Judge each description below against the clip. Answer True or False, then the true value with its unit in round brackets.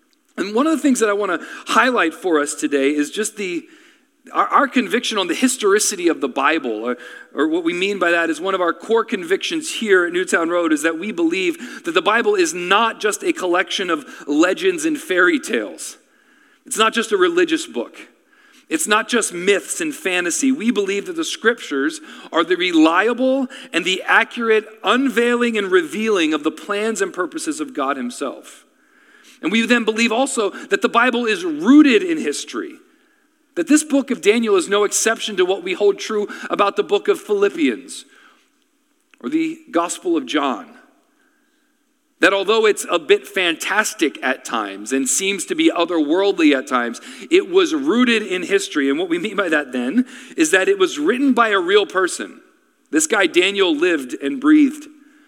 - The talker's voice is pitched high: True (270 Hz)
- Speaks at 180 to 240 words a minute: True (185 wpm)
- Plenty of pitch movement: True (8.3 semitones)